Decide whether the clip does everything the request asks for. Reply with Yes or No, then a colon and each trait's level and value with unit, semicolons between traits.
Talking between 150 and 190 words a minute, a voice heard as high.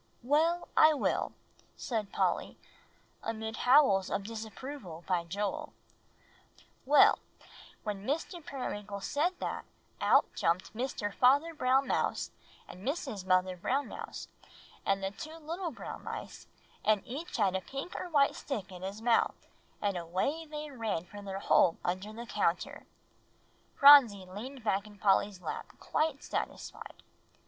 No: average, 140 wpm; high, 220 Hz